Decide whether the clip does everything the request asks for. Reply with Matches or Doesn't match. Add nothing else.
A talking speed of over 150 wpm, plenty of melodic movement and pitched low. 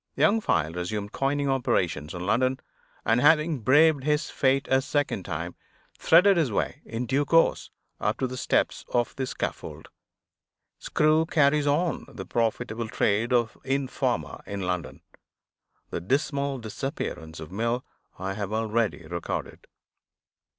Doesn't match